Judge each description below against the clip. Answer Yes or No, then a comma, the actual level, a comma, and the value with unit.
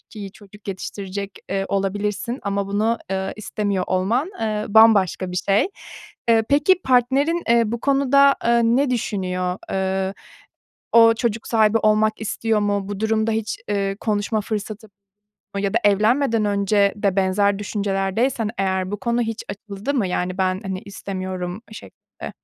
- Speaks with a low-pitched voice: No, high, 205 Hz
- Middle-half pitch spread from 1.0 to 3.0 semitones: Yes, narrow, 2.6 semitones